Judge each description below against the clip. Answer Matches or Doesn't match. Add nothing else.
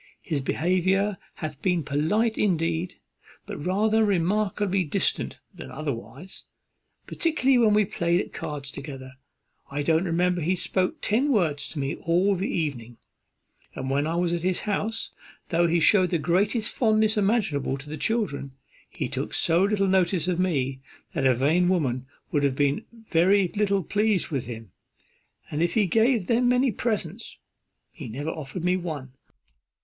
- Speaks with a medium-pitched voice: Matches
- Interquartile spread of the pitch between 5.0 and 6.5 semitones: Matches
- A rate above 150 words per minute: Matches